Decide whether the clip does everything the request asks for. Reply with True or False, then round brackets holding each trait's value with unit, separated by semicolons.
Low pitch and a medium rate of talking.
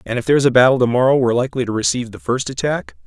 False (115 Hz; 275 wpm)